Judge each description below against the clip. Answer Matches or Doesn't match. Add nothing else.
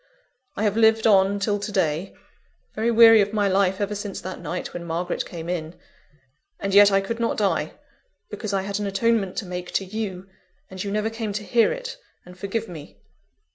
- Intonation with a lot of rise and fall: Doesn't match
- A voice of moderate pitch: Doesn't match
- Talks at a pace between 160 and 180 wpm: Doesn't match